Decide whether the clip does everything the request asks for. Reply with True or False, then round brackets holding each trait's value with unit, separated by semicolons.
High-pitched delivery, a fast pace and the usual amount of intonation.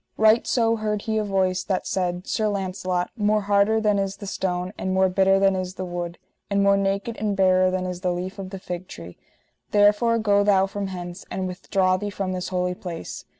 False (195 Hz; 215 wpm; 1.8 semitones)